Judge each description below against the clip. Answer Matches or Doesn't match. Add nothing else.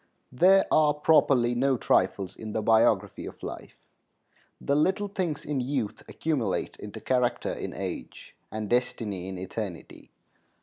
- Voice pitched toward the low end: Matches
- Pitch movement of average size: Doesn't match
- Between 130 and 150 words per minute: Matches